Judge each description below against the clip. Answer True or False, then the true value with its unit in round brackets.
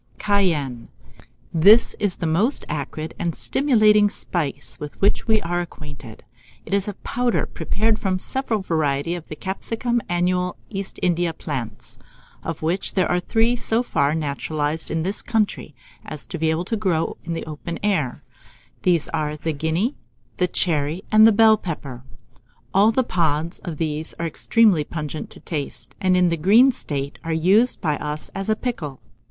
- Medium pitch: True (175 Hz)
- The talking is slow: False (170 wpm)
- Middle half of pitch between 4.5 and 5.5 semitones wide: True (5.1 semitones)